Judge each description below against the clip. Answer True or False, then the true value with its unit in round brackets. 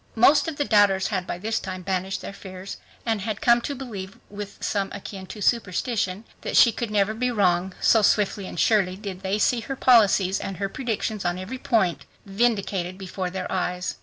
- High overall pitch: True (200 Hz)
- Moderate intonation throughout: True (3.1 semitones)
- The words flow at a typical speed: True (195 wpm)